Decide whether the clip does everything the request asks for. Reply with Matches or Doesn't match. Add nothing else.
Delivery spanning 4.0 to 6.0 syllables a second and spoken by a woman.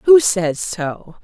Doesn't match